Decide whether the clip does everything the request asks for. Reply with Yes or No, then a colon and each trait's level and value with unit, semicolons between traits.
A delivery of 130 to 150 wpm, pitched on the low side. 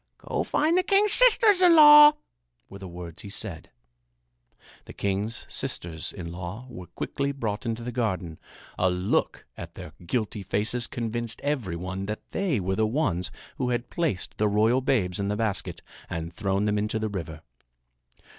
No: average, 175 wpm; low, 105 Hz